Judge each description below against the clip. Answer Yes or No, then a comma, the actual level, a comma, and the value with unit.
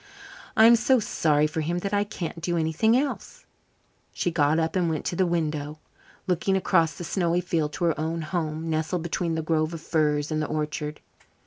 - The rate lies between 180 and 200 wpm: Yes, average, 195 wpm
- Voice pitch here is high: No, medium, 165 Hz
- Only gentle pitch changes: Yes, narrow, 2.3 semitones